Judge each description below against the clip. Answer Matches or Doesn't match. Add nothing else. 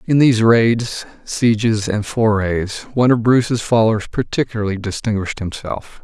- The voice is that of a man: Matches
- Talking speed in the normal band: Doesn't match